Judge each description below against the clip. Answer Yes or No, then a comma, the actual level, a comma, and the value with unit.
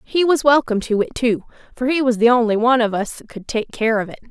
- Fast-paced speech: Yes, fast, 280 wpm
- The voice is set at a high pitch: Yes, high, 240 Hz